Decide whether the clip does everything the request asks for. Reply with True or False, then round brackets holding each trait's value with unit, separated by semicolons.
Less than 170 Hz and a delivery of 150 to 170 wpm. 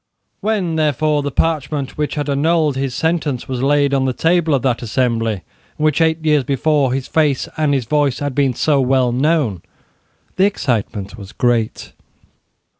True (140 Hz; 165 wpm)